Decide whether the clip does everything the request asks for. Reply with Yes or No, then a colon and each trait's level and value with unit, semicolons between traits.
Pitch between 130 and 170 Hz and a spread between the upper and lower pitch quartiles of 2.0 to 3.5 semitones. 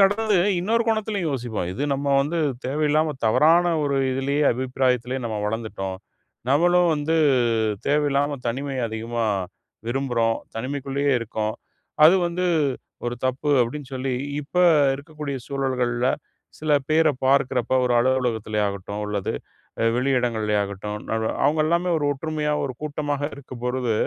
No: low, 135 Hz; average, 4.1 semitones